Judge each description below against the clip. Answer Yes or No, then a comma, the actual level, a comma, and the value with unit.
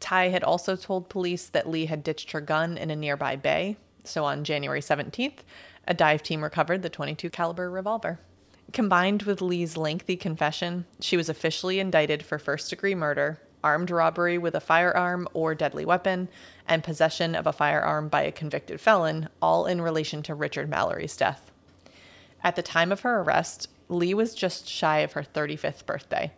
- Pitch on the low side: No, medium, 165 Hz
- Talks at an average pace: Yes, average, 180 wpm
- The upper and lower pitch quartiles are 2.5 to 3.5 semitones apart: Yes, average, 2.9 semitones